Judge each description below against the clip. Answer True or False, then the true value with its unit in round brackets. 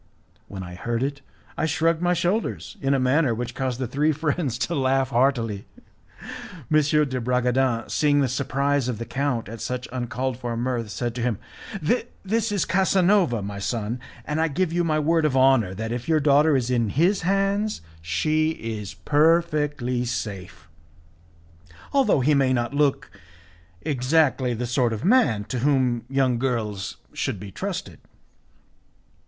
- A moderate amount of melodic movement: True (4.6 semitones)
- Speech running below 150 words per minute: False (160 wpm)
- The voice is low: True (130 Hz)